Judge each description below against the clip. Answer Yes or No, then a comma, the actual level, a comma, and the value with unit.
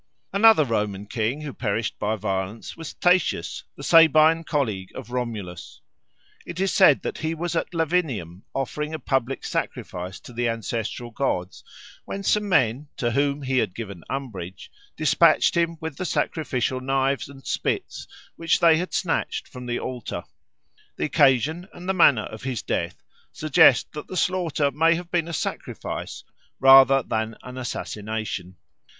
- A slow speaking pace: No, average, 155 wpm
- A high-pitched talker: No, low, 135 Hz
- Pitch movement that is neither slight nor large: No, wide, 6.5 semitones